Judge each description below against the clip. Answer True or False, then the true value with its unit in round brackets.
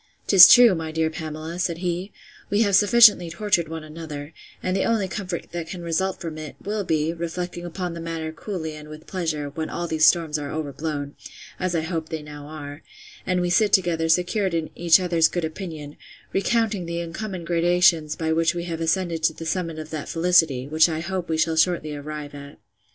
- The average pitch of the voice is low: False (165 Hz)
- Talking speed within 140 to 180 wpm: False (200 wpm)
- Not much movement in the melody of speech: True (2.3 semitones)